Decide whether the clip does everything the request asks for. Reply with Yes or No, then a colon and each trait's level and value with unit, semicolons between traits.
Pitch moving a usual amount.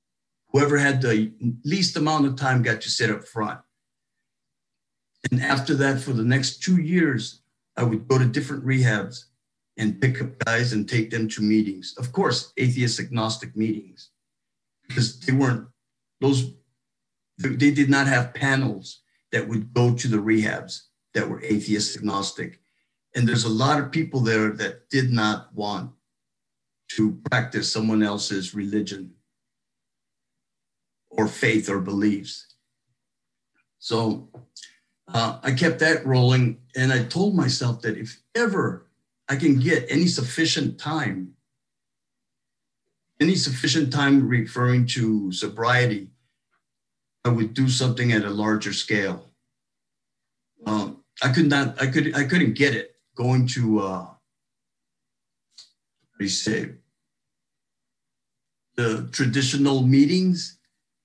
Yes: average, 4.3 semitones